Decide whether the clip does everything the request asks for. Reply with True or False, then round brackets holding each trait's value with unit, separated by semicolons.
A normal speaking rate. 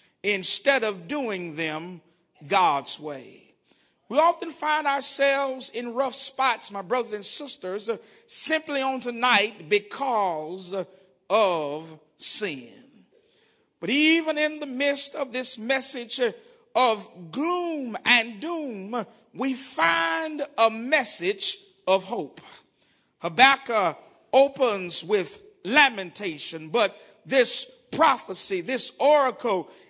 False (100 wpm)